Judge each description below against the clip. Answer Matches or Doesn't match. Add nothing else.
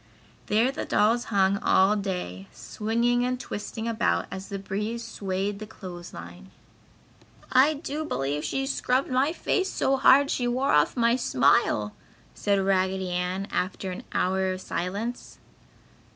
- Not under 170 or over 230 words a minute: Doesn't match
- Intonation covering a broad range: Doesn't match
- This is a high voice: Matches